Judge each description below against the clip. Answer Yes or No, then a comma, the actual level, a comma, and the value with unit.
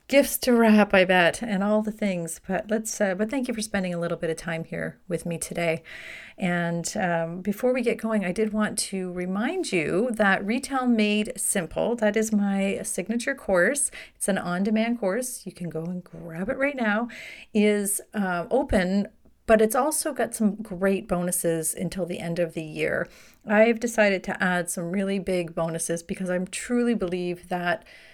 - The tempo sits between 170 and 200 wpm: Yes, average, 190 wpm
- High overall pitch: Yes, high, 195 Hz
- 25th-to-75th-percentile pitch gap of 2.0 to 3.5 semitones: No, average, 3.9 semitones